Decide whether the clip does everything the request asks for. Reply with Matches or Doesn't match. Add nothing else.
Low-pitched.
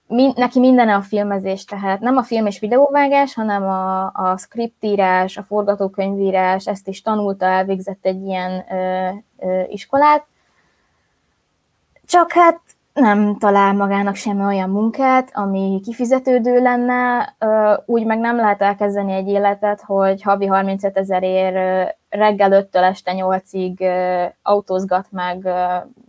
Doesn't match